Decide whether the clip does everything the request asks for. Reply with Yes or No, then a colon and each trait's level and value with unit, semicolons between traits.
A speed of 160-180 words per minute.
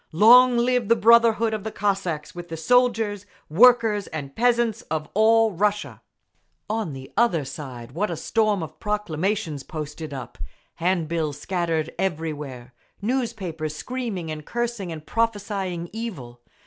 No: slow, 135 wpm